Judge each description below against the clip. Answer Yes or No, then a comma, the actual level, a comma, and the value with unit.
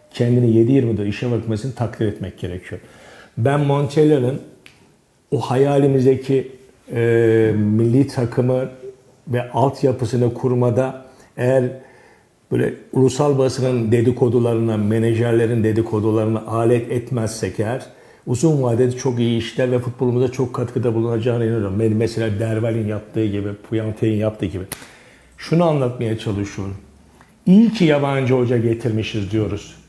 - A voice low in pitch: Yes, low, 120 Hz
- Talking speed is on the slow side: No, average, 110 wpm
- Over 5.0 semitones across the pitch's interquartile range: No, average, 2.8 semitones